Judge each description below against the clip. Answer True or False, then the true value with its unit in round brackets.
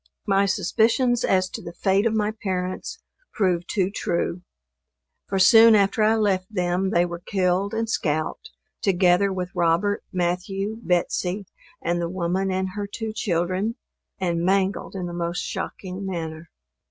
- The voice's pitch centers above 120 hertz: True (190 Hz)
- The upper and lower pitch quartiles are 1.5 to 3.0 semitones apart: True (2.5 semitones)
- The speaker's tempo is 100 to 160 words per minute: True (150 wpm)